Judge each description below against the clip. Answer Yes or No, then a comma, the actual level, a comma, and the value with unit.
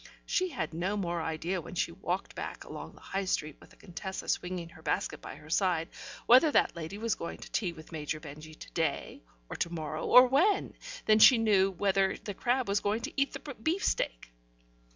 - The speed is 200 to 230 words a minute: Yes, fast, 205 wpm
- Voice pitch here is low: No, medium, 185 Hz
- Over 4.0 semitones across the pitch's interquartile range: Yes, average, 5.2 semitones